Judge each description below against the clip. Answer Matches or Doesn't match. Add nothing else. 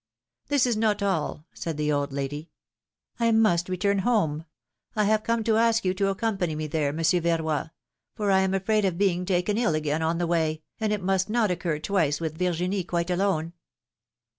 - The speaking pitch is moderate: Matches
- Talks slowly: Doesn't match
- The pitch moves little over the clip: Doesn't match